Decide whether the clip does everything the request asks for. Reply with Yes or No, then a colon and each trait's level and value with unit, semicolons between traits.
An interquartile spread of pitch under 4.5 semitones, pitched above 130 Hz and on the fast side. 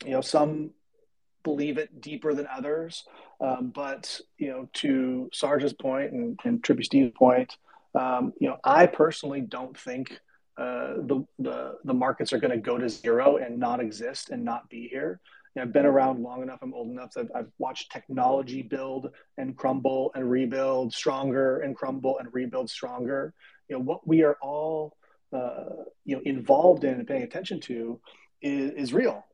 No: average, 2.9 semitones; medium, 140 Hz; average, 185 wpm